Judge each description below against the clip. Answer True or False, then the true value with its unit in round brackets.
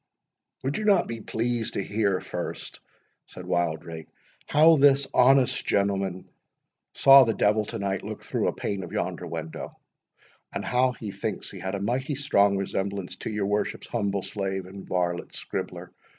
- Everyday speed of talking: True (165 wpm)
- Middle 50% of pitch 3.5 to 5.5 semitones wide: True (4.3 semitones)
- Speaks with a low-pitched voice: True (100 Hz)